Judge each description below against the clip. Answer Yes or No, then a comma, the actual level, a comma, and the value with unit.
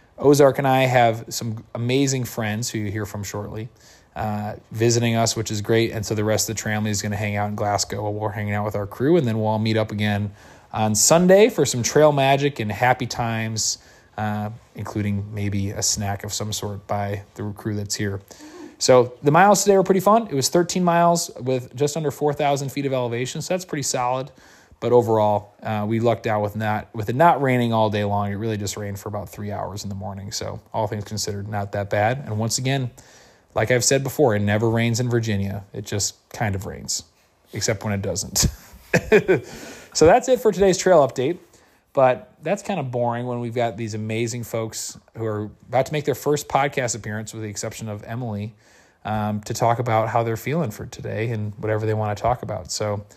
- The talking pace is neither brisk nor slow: No, fast, 220 wpm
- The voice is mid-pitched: No, low, 110 Hz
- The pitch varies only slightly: No, average, 3.3 semitones